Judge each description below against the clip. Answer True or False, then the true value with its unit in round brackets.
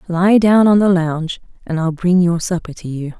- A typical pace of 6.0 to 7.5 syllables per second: False (5.1 syllables/s)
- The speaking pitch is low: False (175 Hz)